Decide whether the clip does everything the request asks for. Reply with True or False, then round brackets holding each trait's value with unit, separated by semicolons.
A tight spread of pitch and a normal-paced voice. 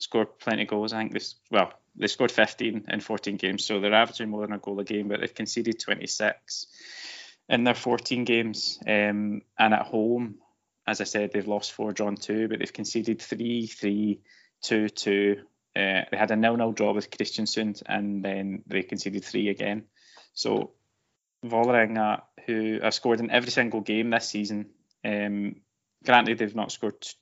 True (1.6 semitones; 180 wpm)